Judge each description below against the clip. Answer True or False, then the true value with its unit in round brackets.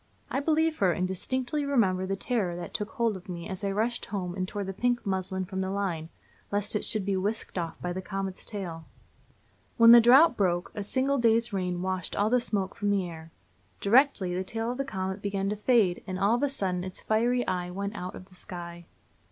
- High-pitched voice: True (195 Hz)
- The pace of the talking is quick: True (225 wpm)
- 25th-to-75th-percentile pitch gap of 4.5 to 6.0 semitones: False (3.9 semitones)